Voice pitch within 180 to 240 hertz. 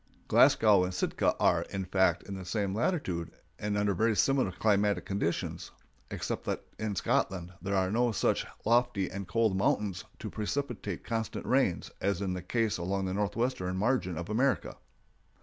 No: low, 100 Hz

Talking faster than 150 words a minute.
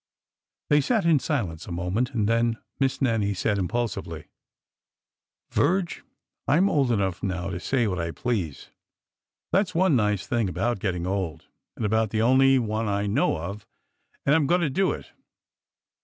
Yes: average, 170 wpm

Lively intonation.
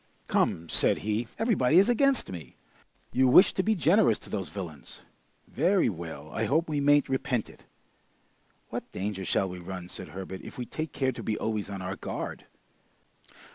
Yes: wide, 8.7 semitones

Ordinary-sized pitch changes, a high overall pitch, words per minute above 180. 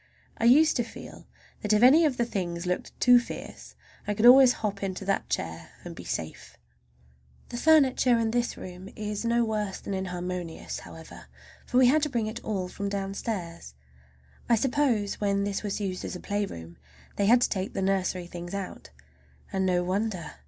Yes: average, 4.3 semitones; high, 205 Hz; average, 190 wpm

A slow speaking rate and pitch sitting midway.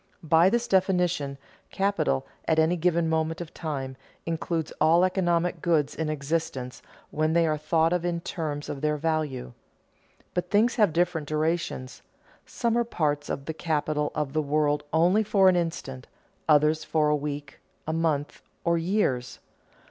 No: average, 155 wpm; medium, 160 Hz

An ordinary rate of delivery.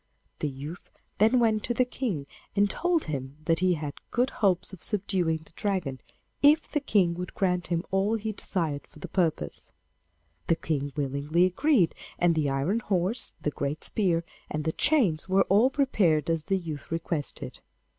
Yes: average, 175 wpm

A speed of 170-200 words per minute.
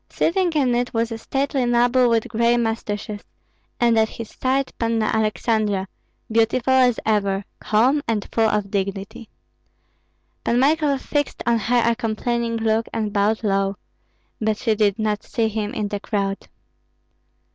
No: average, 150 wpm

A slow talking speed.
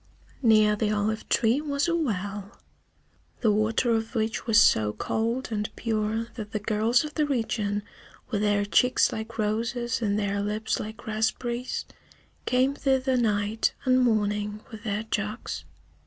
No: average, 150 wpm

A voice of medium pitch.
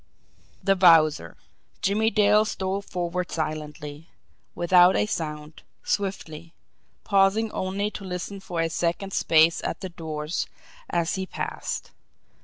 Yes: medium, 180 Hz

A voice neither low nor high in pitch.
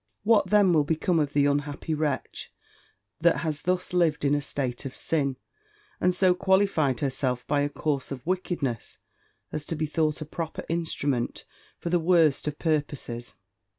Yes: medium, 155 Hz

